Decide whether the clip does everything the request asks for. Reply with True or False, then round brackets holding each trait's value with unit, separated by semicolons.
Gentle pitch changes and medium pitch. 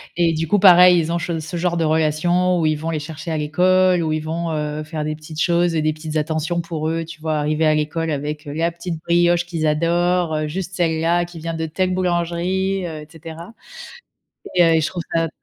True (1.9 semitones; 165 Hz)